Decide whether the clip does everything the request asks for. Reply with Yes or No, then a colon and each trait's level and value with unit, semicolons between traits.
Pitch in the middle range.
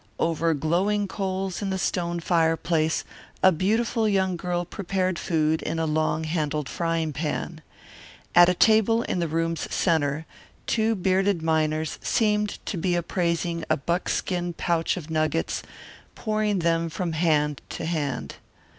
Yes: medium, 170 Hz